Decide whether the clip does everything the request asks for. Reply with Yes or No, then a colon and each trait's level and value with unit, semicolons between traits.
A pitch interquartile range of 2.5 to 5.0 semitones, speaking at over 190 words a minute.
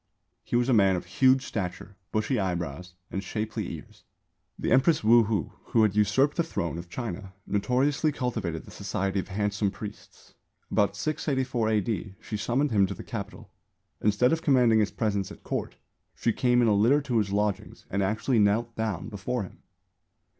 No: average, 3.8 semitones; average, 175 wpm